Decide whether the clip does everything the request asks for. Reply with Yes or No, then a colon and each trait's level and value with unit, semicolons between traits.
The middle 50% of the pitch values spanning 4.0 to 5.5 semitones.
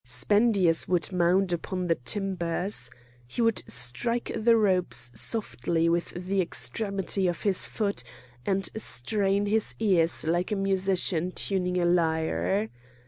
No: average, 3.1 semitones